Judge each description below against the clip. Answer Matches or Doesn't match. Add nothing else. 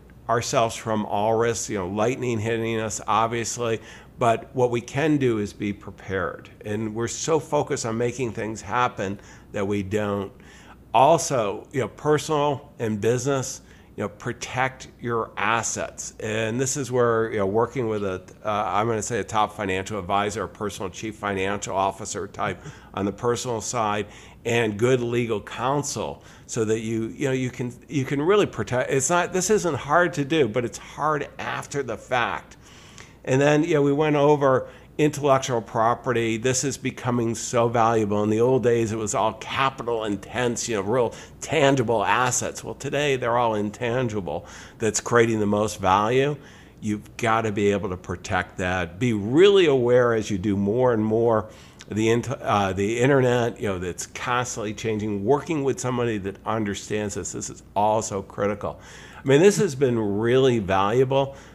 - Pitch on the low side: Matches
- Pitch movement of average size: Matches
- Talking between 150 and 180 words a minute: Matches